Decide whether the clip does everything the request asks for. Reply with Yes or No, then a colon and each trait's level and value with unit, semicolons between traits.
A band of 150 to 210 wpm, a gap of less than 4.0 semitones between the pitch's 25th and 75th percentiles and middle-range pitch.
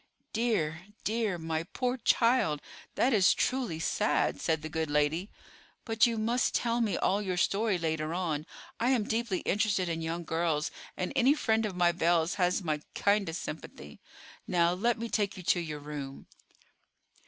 No: average, 165 wpm; wide, 5.5 semitones; medium, 180 Hz